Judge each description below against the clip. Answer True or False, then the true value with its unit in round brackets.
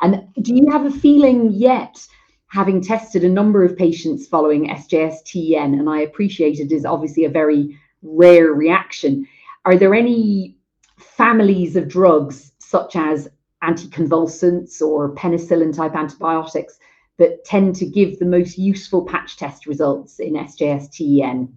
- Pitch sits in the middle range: True (170 Hz)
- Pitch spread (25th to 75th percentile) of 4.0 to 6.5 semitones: True (4.3 semitones)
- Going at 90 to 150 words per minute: True (140 wpm)